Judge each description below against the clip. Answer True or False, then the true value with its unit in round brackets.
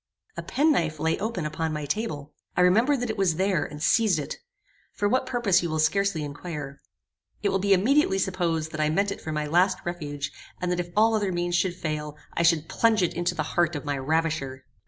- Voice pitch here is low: False (175 Hz)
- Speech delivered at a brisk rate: True (220 wpm)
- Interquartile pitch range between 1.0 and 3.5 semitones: False (4.4 semitones)